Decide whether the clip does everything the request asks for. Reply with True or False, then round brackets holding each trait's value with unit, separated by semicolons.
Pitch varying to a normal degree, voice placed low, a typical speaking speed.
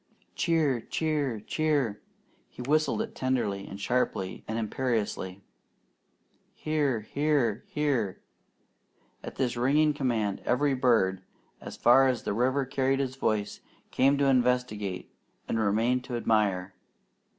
False (4.3 semitones; 125 Hz; 120 wpm)